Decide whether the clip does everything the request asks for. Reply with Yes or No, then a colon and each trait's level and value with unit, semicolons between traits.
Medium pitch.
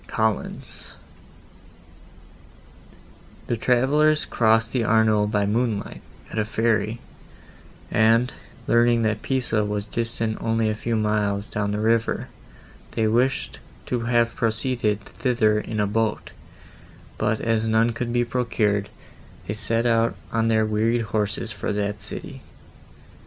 No: low, 110 Hz